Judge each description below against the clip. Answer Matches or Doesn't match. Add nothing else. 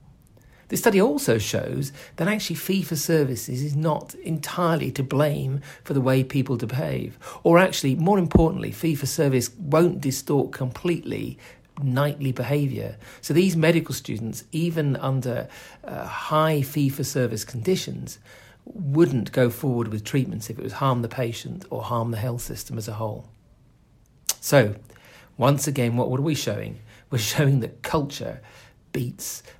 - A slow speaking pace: Doesn't match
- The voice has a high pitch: Doesn't match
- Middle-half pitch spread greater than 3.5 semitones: Matches